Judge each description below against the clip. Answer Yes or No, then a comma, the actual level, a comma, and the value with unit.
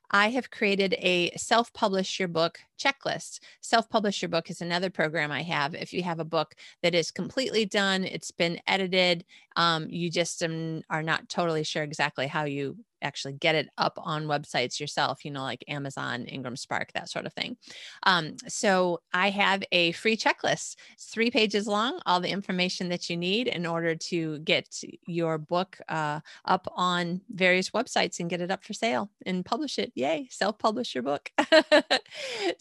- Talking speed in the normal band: Yes, average, 180 wpm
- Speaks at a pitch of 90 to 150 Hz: No, medium, 180 Hz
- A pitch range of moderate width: Yes, average, 4.5 semitones